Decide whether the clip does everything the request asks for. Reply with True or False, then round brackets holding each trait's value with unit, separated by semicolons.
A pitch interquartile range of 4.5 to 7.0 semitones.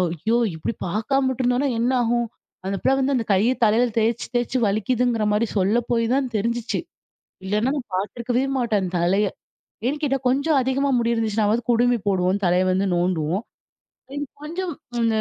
False (3.9 semitones)